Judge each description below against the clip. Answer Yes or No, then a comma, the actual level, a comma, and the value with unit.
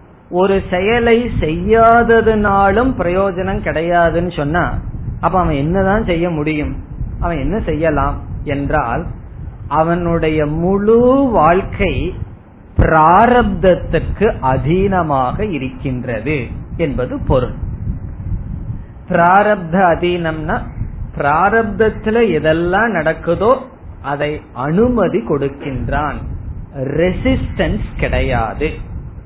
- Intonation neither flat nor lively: No, wide, 6.6 semitones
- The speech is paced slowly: Yes, slow, 70 wpm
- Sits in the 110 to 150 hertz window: No, medium, 165 Hz